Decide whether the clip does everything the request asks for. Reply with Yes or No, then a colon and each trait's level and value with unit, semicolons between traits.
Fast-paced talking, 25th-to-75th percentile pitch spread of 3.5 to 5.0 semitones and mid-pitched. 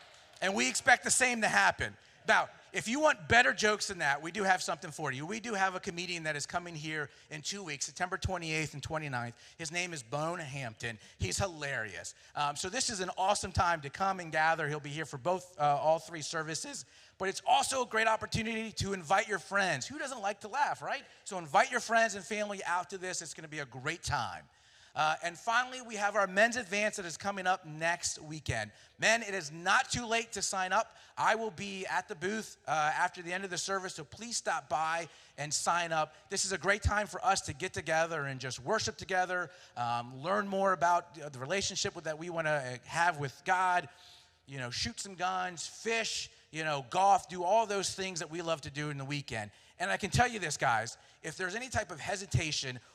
Yes: fast, 225 wpm; average, 4.6 semitones; medium, 180 Hz